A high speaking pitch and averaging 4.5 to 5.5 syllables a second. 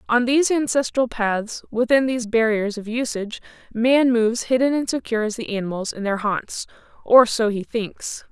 Yes: high, 230 Hz; 5.2 syllables/s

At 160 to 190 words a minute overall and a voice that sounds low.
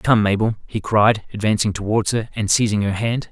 No: average, 200 wpm; low, 105 Hz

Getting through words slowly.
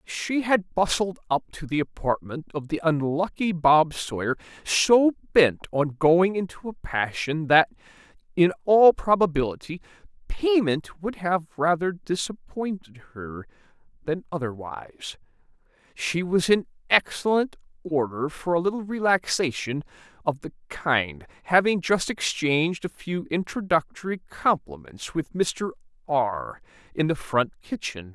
Yes: slow, 120 wpm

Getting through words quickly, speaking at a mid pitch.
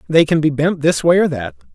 Yes: fast, 275 wpm; medium, 145 Hz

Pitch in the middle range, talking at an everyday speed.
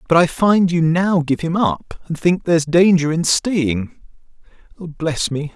Yes: medium, 165 Hz; average, 175 wpm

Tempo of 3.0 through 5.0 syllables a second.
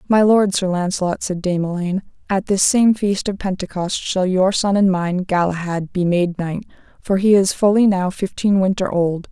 Yes: 4.8 syllables/s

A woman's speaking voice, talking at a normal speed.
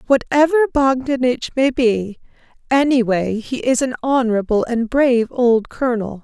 No: female; slow, 125 wpm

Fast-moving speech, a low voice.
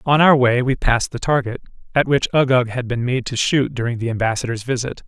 Yes: fast, 225 wpm; low, 125 Hz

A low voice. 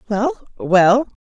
No: high, 210 Hz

